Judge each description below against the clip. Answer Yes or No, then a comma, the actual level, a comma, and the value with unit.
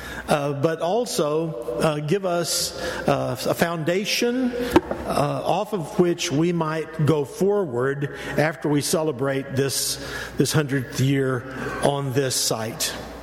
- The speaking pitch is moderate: Yes, medium, 155 Hz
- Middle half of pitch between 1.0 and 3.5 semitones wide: No, average, 4.0 semitones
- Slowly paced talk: Yes, slow, 120 wpm